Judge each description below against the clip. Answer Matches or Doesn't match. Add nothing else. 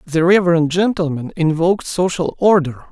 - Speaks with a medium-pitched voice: Matches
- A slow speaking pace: Matches